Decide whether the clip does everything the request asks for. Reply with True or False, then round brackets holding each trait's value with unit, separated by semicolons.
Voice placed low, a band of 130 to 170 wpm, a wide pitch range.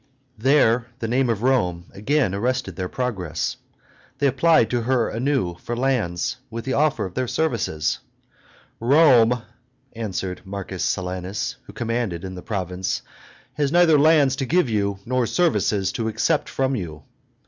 True (115 Hz; 150 wpm; 5.7 semitones)